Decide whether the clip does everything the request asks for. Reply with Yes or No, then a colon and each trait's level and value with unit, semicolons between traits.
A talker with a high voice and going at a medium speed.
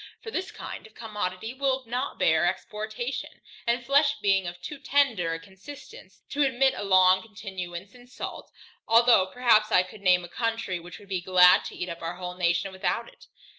Yes: high, 205 Hz; average, 190 wpm